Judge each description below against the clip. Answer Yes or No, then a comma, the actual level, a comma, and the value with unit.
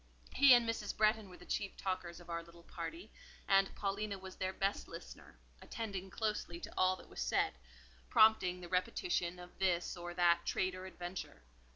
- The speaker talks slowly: No, average, 180 wpm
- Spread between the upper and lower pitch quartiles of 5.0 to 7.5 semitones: No, average, 2.8 semitones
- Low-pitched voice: No, medium, 185 Hz